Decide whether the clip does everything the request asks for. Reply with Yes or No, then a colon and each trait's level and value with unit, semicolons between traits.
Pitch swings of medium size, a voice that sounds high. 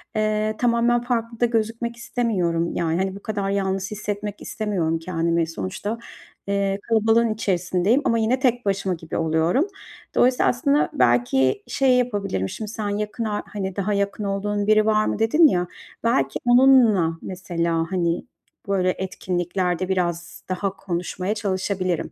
Yes: average, 3.9 semitones; high, 200 Hz